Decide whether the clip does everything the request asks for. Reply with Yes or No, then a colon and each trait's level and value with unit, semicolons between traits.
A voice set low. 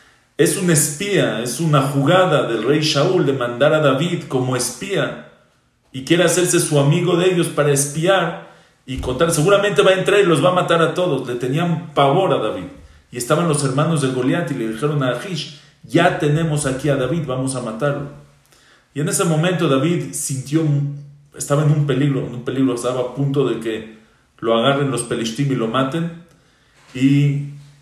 No: medium, 145 Hz